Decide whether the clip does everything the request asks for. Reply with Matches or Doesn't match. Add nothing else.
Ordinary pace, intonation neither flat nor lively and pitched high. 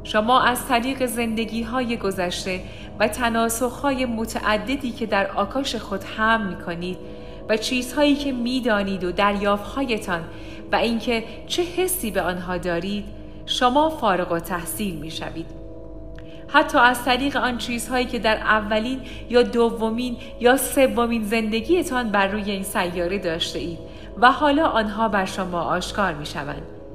Matches